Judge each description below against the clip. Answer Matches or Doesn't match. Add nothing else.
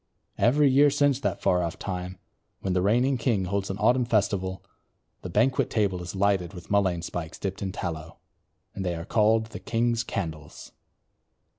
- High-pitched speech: Doesn't match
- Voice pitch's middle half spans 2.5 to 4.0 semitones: Doesn't match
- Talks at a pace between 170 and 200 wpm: Matches